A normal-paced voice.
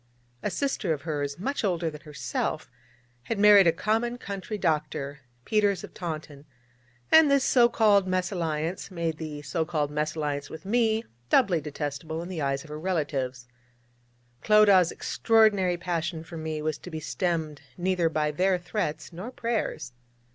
Yes: average, 155 wpm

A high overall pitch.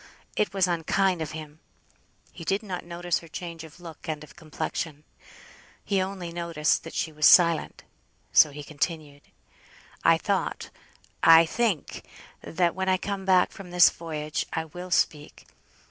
No: medium, 170 Hz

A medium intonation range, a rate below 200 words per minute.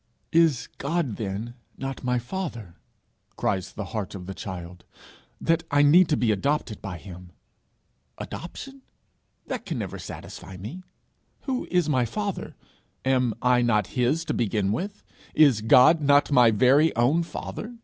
No: wide, 7.1 semitones; average, 150 wpm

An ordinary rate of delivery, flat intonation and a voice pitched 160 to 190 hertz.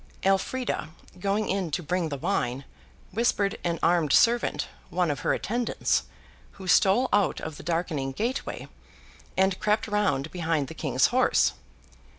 No: average, 150 wpm; average, 4.6 semitones; medium, 185 Hz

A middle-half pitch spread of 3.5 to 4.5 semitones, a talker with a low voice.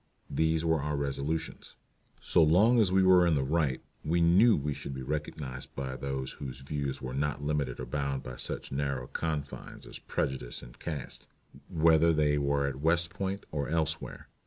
No: average, 3.1 semitones; very low, 75 Hz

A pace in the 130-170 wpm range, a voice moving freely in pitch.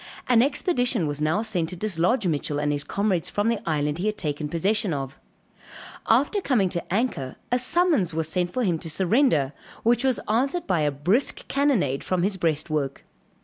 No: average, 185 wpm; wide, 7.3 semitones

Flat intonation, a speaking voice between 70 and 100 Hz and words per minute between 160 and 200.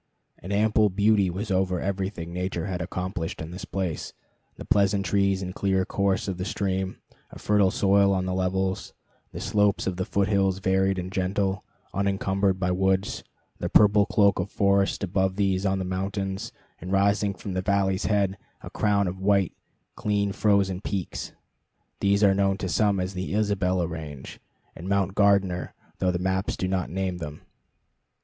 Yes: narrow, 1.3 semitones; very low, 95 Hz; average, 170 wpm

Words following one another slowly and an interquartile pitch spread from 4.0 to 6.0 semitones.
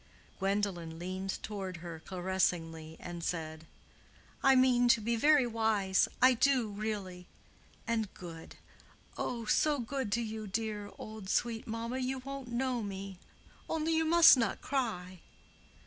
Yes: slow, 130 wpm; average, 4.9 semitones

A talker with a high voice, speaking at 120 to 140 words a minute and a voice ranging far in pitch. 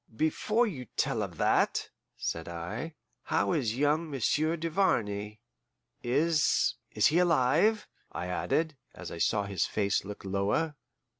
No: medium, 140 Hz; slow, 135 wpm; wide, 8.1 semitones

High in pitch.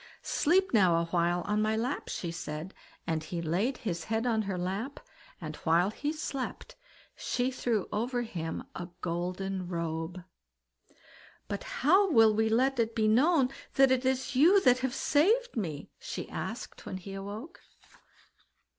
Yes: high, 220 Hz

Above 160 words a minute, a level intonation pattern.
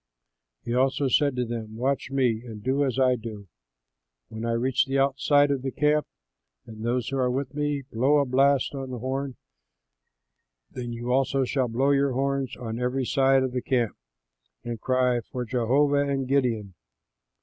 Yes: average, 175 wpm; narrow, 2.3 semitones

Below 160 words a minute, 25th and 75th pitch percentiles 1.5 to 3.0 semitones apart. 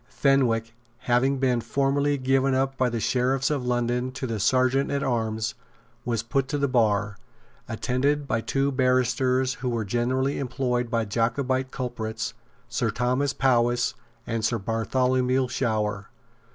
Yes: average, 140 wpm; narrow, 2.4 semitones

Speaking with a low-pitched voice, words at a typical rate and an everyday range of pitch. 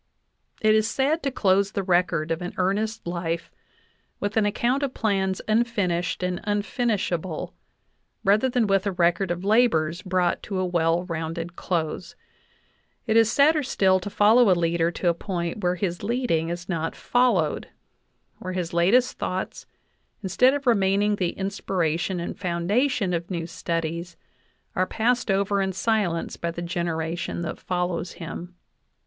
No: medium, 185 Hz; average, 160 wpm; average, 3.8 semitones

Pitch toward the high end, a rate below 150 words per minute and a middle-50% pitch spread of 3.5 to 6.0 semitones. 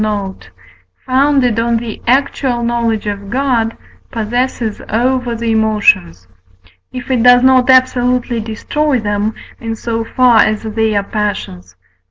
No: high, 230 Hz; slow, 135 wpm; average, 2.7 semitones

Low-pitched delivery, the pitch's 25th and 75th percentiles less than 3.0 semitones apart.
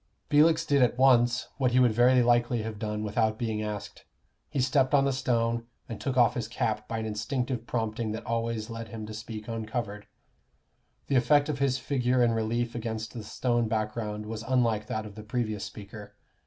Yes: low, 115 Hz; narrow, 2.5 semitones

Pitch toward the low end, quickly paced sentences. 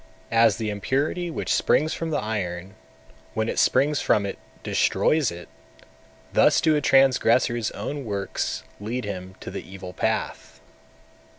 No: low, 115 Hz; average, 150 wpm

